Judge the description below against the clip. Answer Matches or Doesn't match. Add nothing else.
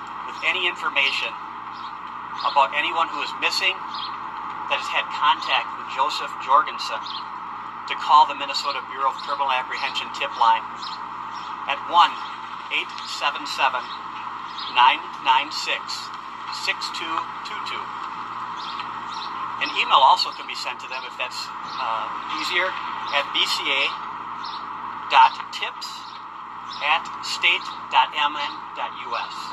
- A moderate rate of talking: Doesn't match